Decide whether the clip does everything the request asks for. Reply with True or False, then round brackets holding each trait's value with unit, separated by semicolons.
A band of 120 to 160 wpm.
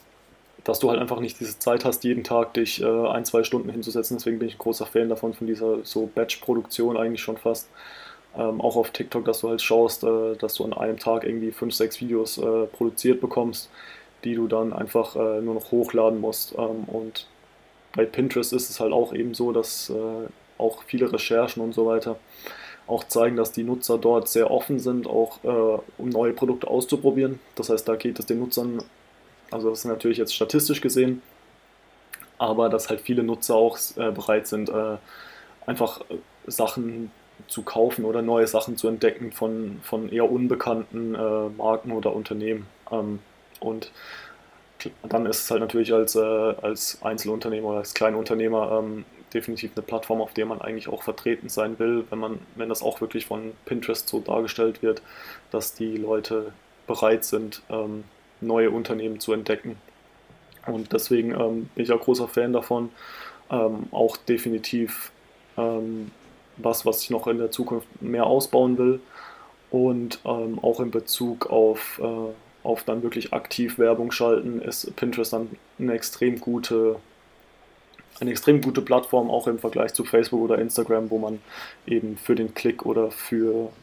False (170 wpm)